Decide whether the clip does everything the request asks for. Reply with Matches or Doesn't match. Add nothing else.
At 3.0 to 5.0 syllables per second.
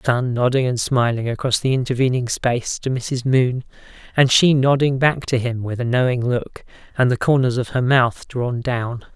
Matches